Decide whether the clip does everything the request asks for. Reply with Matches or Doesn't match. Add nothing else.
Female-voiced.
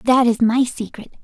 Matches